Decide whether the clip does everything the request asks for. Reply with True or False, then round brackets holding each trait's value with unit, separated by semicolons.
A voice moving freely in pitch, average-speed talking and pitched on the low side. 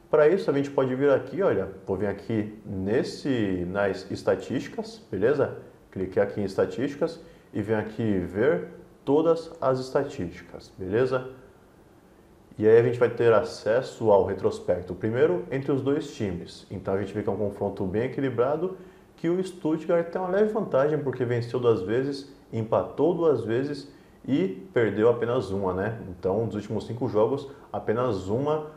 True (7.8 semitones; 155 wpm; 130 Hz)